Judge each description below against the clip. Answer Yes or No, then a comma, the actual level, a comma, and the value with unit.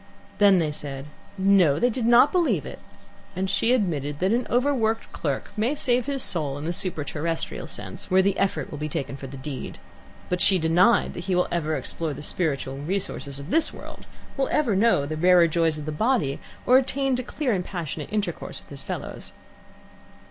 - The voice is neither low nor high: Yes, medium, 180 Hz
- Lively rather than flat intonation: Yes, wide, 7.1 semitones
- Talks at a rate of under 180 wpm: No, average, 195 wpm